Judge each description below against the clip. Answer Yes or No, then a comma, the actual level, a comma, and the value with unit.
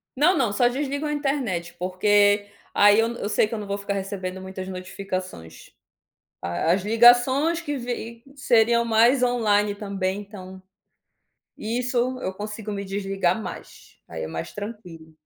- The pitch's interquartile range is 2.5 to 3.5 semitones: No, average, 4.2 semitones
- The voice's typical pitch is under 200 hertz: No, high, 210 Hz